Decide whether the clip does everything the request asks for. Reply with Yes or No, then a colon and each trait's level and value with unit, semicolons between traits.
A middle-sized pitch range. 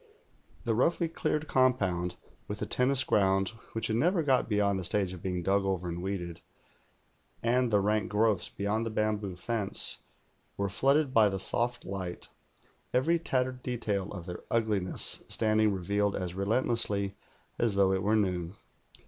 Yes: average, 3.6 semitones